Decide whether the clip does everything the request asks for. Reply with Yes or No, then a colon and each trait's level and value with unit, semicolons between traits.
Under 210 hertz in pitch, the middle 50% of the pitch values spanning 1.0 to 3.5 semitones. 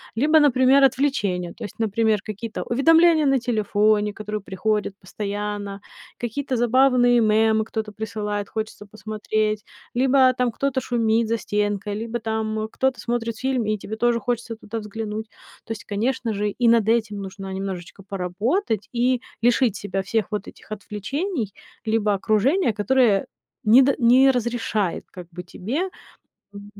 No: high, 220 Hz; average, 2.9 semitones